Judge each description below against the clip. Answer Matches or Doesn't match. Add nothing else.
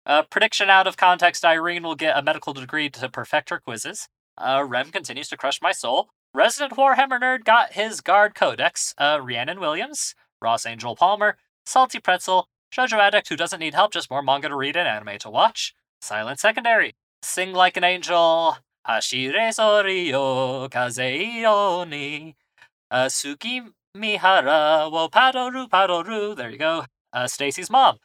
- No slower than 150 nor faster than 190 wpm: Matches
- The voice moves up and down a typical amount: Doesn't match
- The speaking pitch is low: Doesn't match